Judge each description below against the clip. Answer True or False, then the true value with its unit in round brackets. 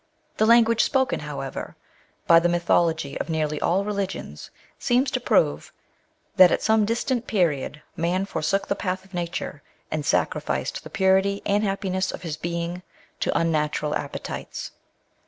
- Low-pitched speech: False (185 Hz)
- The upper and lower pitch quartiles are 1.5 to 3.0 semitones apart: False (3.8 semitones)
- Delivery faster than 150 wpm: False (145 wpm)